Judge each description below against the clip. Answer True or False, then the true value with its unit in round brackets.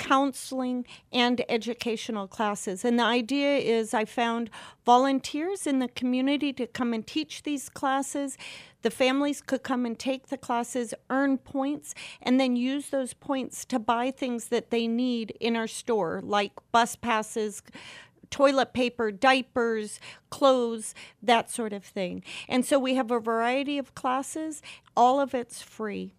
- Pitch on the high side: True (245 Hz)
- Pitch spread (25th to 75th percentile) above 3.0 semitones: False (2.7 semitones)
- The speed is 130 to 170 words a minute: True (155 wpm)